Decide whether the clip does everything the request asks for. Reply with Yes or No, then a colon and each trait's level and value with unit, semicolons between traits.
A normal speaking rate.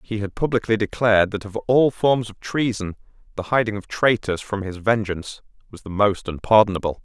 Yes: average, 180 wpm